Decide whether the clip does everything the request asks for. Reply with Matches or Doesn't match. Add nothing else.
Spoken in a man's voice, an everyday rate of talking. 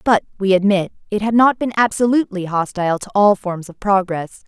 Doesn't match